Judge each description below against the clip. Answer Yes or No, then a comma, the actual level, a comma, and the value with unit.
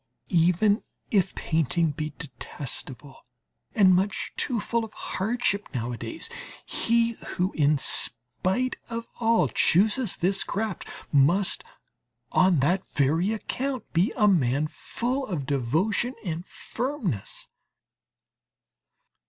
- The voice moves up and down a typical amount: No, wide, 6.7 semitones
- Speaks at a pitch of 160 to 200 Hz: Yes, medium, 185 Hz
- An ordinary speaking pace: No, slow, 105 wpm